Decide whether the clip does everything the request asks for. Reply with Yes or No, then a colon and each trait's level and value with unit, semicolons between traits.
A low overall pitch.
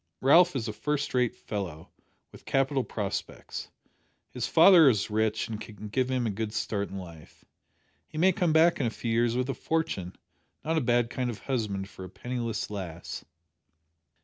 Yes: low, 115 Hz